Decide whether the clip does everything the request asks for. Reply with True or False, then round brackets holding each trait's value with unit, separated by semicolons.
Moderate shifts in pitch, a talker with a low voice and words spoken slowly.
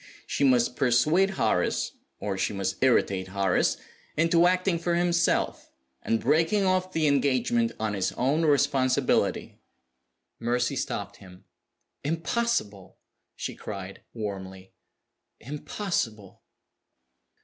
False (8.4 semitones; 130 Hz; 105 wpm)